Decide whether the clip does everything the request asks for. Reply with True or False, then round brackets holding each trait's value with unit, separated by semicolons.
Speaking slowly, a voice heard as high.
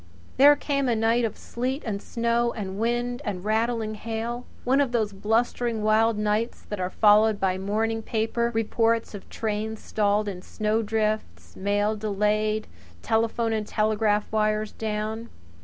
False (145 wpm; 220 Hz)